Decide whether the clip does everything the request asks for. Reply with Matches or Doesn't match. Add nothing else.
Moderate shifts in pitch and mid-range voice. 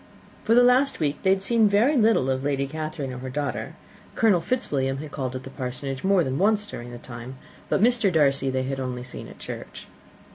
Doesn't match